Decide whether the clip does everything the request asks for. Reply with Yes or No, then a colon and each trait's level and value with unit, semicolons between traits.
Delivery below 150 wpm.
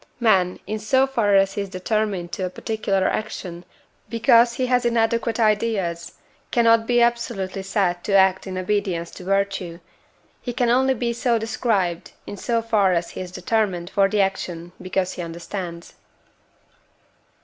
No: average, 160 wpm